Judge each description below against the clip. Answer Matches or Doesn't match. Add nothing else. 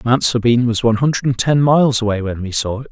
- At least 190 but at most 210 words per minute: Doesn't match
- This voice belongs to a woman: Doesn't match